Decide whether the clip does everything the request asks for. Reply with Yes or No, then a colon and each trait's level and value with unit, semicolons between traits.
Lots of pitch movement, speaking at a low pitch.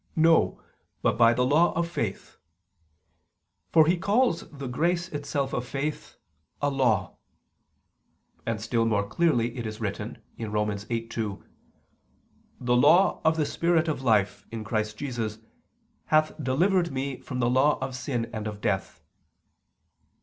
Yes: wide, 5.7 semitones; low, 125 Hz